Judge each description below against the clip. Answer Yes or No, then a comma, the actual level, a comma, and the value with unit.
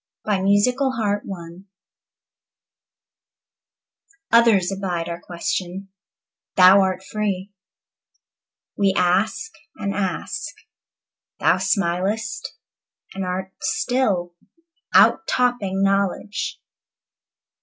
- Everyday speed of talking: No, slow, 75 wpm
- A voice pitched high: Yes, high, 195 Hz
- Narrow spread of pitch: Yes, narrow, 2.2 semitones